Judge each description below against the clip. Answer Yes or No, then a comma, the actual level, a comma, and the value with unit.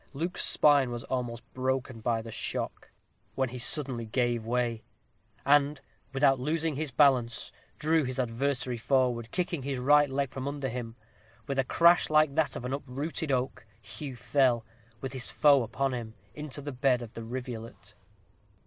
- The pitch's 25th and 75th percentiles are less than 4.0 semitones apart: Yes, average, 2.8 semitones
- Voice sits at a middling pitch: No, low, 130 Hz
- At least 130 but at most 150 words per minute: No, average, 165 wpm